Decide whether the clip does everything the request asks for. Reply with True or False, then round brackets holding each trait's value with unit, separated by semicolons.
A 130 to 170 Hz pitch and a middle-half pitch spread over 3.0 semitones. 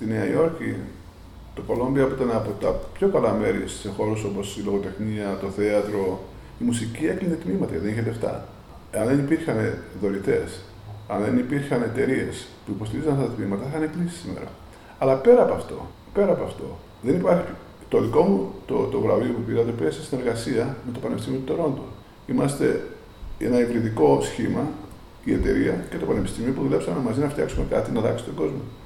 False (110 Hz; 4.7 semitones)